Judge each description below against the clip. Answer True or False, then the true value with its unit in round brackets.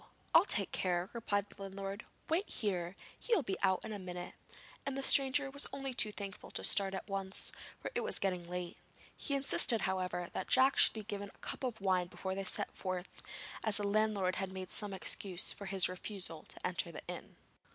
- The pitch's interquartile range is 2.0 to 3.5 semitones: True (2.8 semitones)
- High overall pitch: True (195 Hz)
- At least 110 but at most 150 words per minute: False (205 wpm)